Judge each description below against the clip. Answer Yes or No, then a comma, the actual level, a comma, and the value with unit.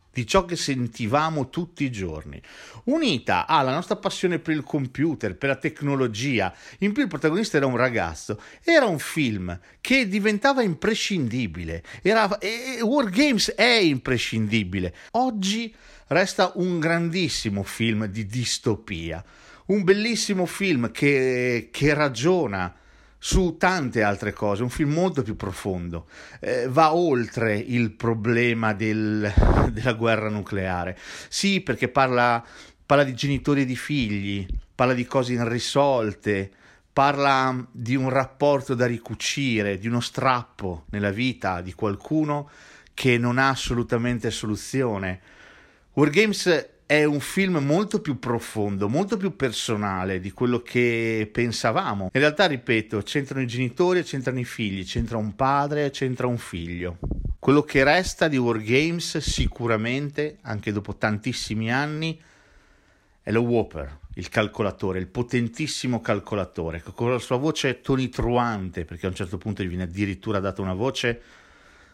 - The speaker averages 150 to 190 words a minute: No, average, 135 wpm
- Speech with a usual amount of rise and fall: No, wide, 6.0 semitones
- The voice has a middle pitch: No, low, 125 Hz